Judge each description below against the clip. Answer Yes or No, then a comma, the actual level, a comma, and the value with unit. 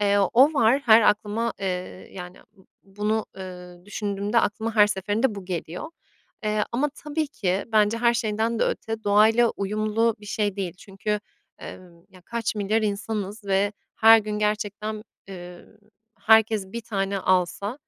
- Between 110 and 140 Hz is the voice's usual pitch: No, high, 210 Hz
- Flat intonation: Yes, narrow, 2.3 semitones